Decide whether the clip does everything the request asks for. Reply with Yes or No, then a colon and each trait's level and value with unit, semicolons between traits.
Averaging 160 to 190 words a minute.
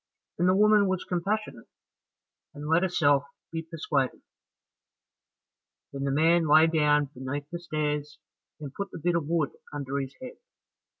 No: average, 145 wpm